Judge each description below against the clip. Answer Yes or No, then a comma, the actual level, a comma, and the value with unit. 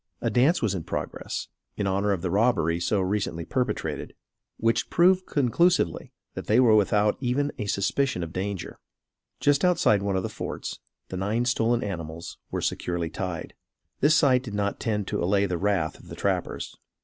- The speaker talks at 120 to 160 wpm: No, average, 175 wpm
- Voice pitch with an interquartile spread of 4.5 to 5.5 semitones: Yes, average, 4.9 semitones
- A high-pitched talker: No, low, 105 Hz